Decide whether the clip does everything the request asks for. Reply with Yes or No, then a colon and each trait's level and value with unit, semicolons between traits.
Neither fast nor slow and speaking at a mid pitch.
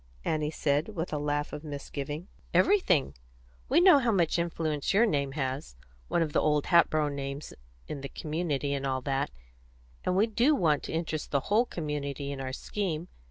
Yes: average, 180 wpm; medium, 150 Hz